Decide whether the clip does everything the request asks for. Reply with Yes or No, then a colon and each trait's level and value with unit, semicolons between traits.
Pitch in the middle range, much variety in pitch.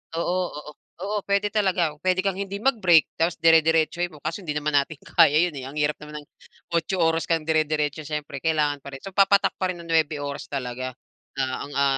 No: medium, 160 Hz; average, 3.2 semitones